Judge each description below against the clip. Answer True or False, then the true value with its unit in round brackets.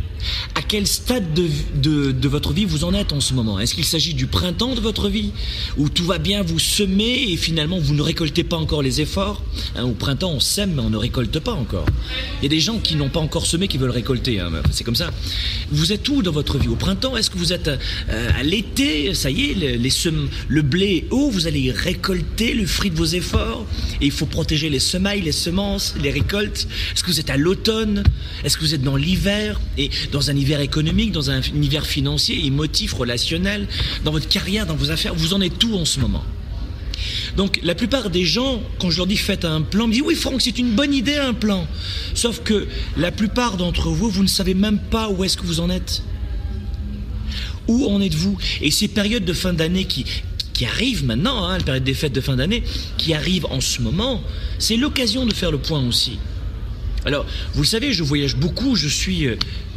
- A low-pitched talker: False (155 Hz)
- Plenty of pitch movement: True (8.3 semitones)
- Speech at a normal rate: False (225 wpm)